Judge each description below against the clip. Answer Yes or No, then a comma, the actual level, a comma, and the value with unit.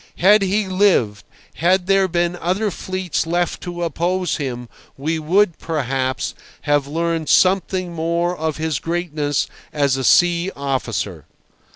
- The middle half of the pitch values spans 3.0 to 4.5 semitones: Yes, average, 4.0 semitones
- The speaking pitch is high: No, medium, 170 Hz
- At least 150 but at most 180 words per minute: No, slow, 135 wpm